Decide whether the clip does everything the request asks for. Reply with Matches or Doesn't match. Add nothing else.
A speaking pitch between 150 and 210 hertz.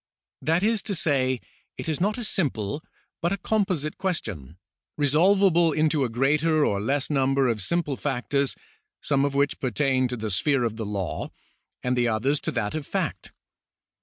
Doesn't match